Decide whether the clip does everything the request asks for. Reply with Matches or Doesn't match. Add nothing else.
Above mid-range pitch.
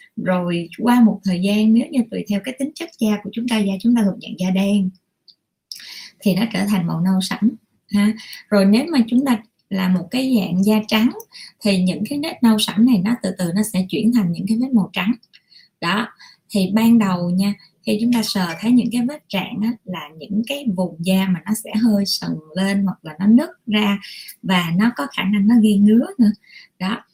Matches